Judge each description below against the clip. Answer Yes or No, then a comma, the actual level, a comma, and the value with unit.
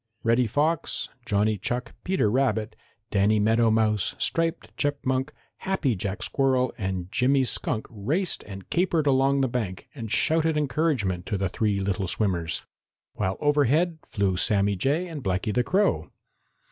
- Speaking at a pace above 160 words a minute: No, average, 145 wpm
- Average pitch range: No, wide, 6.3 semitones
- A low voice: Yes, low, 120 Hz